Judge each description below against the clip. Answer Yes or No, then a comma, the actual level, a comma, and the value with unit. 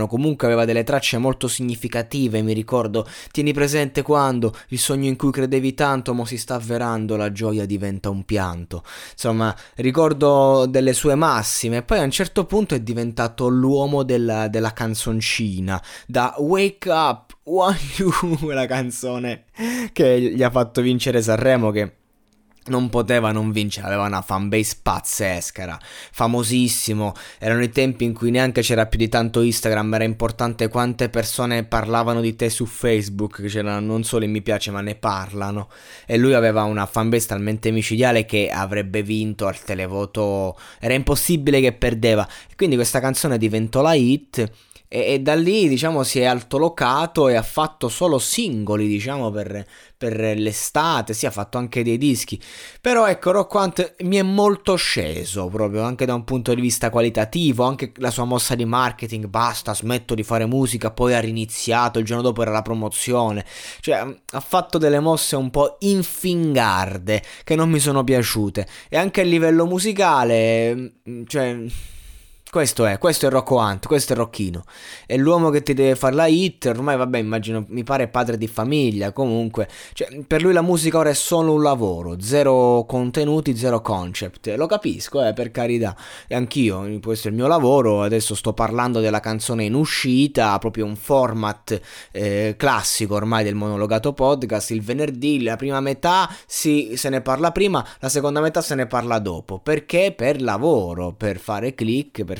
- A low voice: Yes, low, 120 Hz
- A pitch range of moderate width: Yes, average, 4.0 semitones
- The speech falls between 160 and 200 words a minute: Yes, fast, 170 wpm